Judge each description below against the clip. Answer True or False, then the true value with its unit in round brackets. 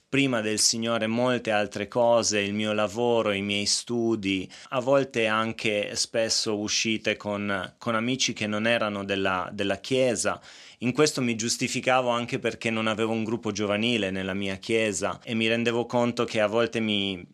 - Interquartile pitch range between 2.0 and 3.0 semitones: True (2.6 semitones)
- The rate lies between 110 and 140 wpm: False (165 wpm)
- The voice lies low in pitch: True (110 Hz)